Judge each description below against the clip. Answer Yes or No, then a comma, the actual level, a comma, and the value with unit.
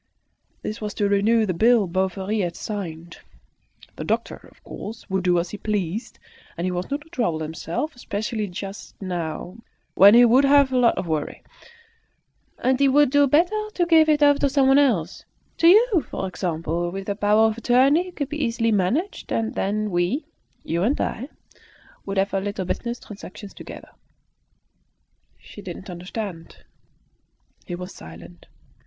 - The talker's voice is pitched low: No, high, 210 Hz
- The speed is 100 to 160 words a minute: No, average, 170 wpm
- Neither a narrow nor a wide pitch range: No, wide, 6.5 semitones